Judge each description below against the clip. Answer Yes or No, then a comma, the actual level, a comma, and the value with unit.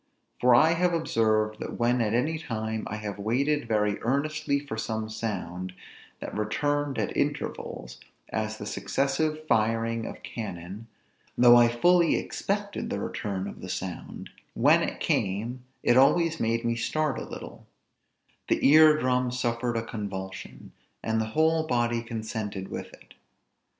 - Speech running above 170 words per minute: No, average, 150 wpm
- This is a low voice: Yes, low, 115 Hz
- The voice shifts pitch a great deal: No, average, 4.7 semitones